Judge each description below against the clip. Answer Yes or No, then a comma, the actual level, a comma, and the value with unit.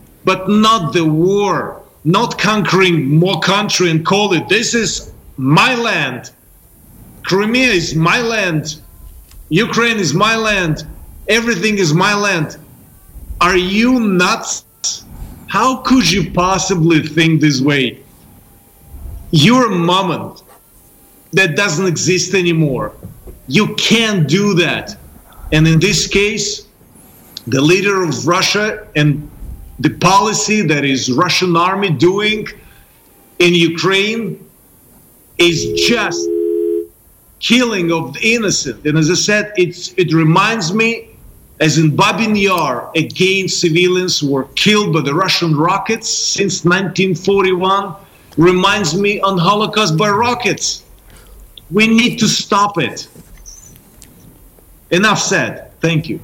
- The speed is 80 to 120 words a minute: Yes, slow, 115 wpm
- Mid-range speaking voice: Yes, medium, 180 Hz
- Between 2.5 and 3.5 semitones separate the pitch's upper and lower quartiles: No, average, 4.6 semitones